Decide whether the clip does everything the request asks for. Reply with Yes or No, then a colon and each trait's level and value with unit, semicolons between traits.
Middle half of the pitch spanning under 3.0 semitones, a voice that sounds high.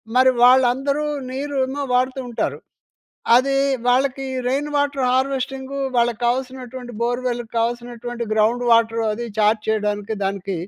Yes: narrow, 2.4 semitones; high, 245 Hz